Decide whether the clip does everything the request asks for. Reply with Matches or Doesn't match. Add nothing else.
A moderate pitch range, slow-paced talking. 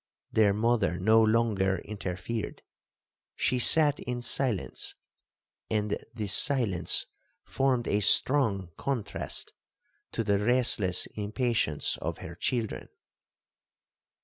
Matches